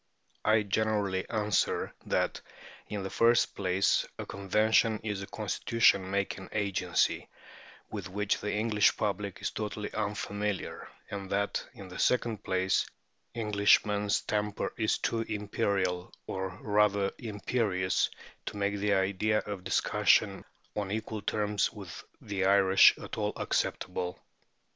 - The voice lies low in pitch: Yes, low, 100 Hz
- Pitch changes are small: Yes, narrow, 1.6 semitones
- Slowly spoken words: Yes, slow, 125 wpm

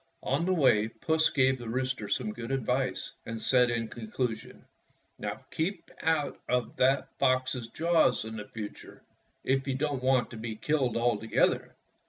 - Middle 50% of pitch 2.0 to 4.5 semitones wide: Yes, average, 2.9 semitones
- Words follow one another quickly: No, average, 155 wpm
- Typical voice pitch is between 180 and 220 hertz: No, low, 130 Hz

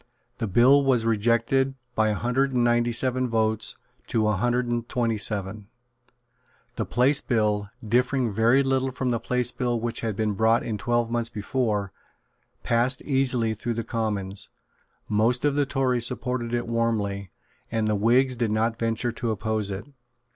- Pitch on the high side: No, low, 115 Hz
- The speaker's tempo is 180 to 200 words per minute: No, average, 165 wpm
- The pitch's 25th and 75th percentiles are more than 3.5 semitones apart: No, narrow, 2.4 semitones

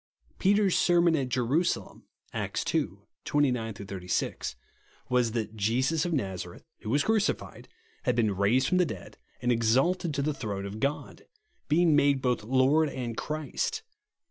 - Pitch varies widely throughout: Yes, wide, 6.0 semitones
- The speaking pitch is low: Yes, low, 130 Hz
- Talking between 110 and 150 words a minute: Yes, average, 145 wpm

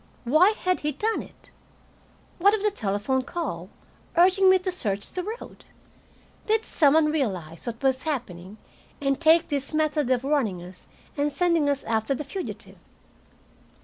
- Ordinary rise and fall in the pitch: No, wide, 6.9 semitones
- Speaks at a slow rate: No, average, 155 wpm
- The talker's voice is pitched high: Yes, very high, 290 Hz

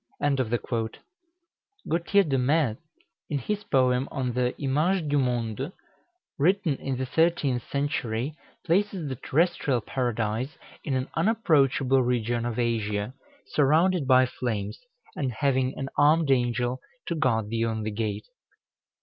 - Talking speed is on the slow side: Yes, slow, 125 wpm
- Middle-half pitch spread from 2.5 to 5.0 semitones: Yes, average, 4.0 semitones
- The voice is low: Yes, low, 130 Hz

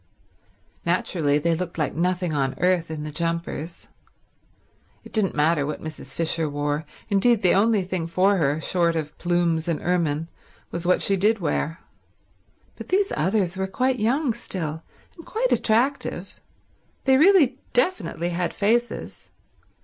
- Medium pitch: Yes, medium, 175 Hz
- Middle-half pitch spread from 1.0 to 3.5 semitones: No, average, 5.2 semitones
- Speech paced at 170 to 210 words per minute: No, average, 145 wpm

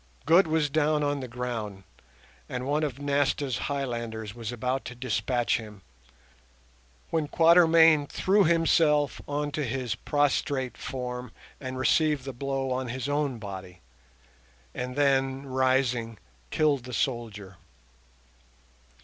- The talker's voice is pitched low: Yes, low, 130 Hz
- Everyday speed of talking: No, slow, 125 wpm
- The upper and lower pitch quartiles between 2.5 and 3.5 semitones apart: Yes, average, 3.2 semitones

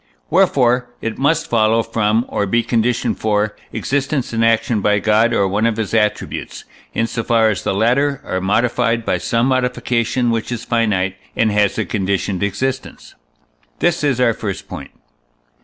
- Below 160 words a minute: No, average, 165 wpm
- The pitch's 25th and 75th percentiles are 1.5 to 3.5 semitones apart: Yes, average, 2.8 semitones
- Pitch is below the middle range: Yes, low, 115 Hz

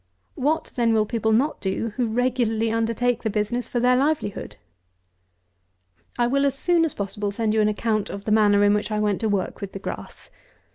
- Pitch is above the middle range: Yes, high, 225 Hz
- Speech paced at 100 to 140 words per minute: No, average, 200 wpm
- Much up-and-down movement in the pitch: No, average, 2.9 semitones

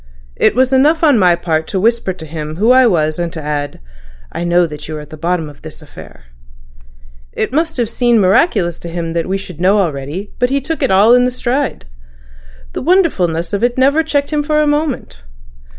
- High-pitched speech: Yes, high, 195 Hz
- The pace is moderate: No, fast, 215 wpm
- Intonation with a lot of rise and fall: Yes, wide, 7.9 semitones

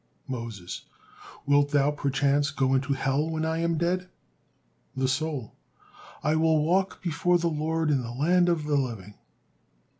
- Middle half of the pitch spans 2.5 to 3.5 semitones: Yes, average, 3.2 semitones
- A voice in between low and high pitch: Yes, medium, 145 Hz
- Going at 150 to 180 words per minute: Yes, average, 155 wpm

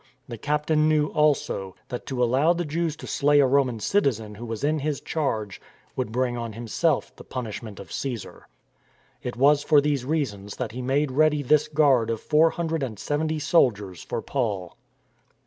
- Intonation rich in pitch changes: No, average, 4.6 semitones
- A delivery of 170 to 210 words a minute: Yes, average, 180 wpm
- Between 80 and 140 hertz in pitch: Yes, low, 135 Hz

